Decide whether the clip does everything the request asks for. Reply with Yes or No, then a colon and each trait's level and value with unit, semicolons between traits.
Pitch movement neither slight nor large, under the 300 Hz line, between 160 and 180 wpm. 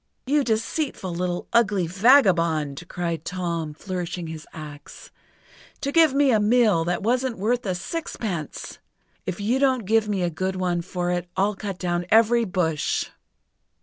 No: average, 4.9 semitones; medium, 185 Hz; average, 150 wpm